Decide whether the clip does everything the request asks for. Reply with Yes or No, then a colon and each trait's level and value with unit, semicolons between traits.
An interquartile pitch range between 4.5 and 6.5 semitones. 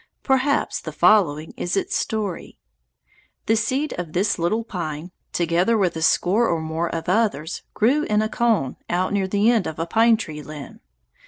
Yes: average, 5.2 semitones